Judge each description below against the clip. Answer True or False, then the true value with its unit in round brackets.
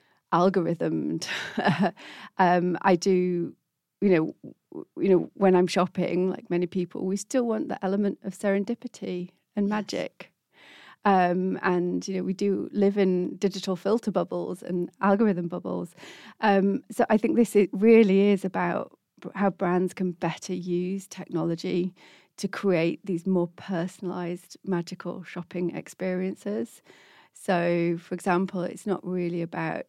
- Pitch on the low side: False (185 Hz)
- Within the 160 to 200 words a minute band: False (135 wpm)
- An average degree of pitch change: False (2.0 semitones)